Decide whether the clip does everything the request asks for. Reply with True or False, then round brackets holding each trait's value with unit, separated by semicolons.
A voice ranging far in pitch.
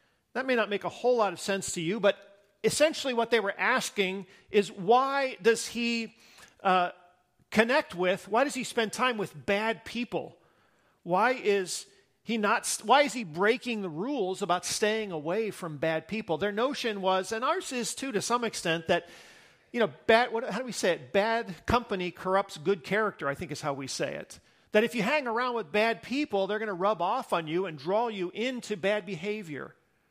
False (3.8 semitones)